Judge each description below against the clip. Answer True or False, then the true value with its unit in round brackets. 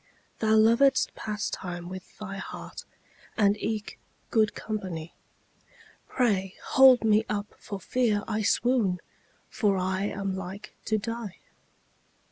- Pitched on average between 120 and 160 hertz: False (210 Hz)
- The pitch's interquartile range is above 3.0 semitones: False (2.7 semitones)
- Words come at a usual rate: False (115 wpm)